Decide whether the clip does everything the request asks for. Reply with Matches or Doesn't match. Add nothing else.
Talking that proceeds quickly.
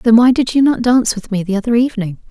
Matches